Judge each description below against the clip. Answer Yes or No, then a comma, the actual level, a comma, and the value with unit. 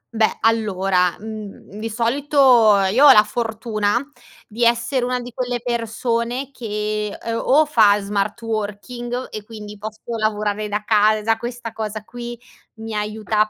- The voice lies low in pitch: No, high, 220 Hz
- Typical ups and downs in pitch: No, narrow, 2.2 semitones